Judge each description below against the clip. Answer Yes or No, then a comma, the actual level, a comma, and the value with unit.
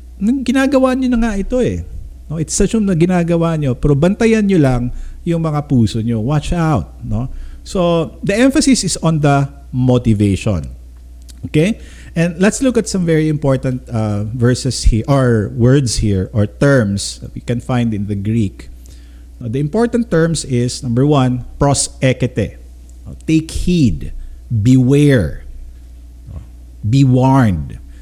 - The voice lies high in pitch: No, low, 130 Hz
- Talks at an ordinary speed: Yes, average, 145 wpm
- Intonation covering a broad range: Yes, wide, 8.1 semitones